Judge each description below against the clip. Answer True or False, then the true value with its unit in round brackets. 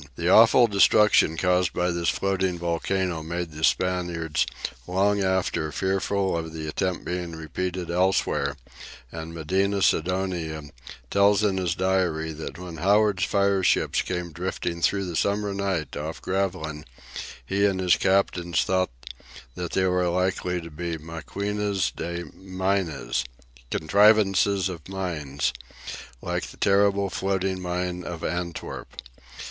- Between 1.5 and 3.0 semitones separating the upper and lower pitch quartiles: True (2.6 semitones)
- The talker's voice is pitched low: True (90 Hz)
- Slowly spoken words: True (130 wpm)